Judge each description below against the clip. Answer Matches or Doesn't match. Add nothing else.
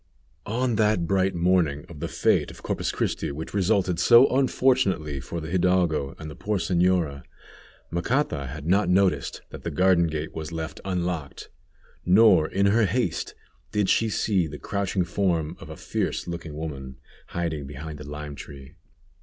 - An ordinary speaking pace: Matches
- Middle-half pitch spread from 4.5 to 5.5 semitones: Doesn't match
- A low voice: Matches